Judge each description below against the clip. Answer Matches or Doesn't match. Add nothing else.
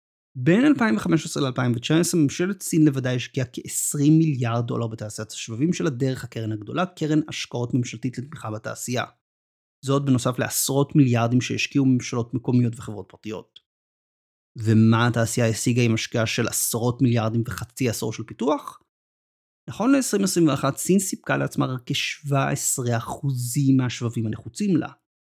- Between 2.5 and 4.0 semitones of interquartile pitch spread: Doesn't match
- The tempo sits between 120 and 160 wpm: Matches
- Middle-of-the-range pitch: Doesn't match